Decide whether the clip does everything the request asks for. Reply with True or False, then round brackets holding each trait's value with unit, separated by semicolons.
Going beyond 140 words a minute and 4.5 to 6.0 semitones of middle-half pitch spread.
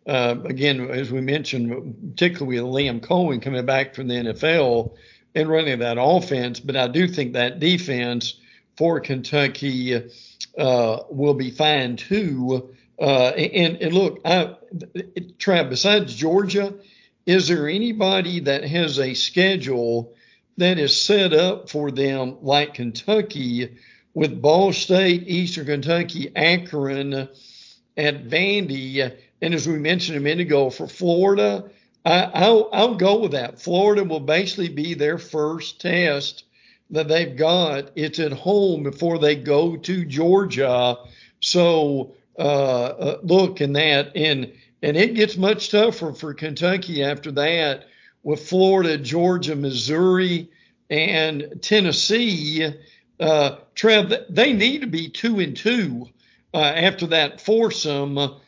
False (135 wpm; 4.9 semitones)